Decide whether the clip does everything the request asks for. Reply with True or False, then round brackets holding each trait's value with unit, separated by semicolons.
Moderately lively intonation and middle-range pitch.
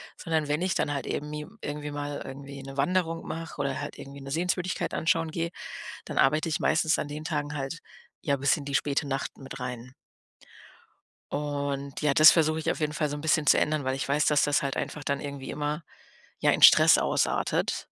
False (2.0 semitones; 145 Hz)